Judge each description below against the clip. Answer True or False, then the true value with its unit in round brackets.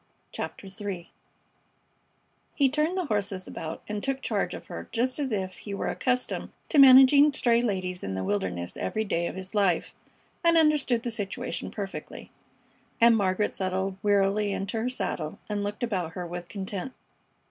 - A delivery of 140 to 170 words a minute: True (165 wpm)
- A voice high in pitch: True (205 Hz)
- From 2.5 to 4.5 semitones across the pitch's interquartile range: False (5.1 semitones)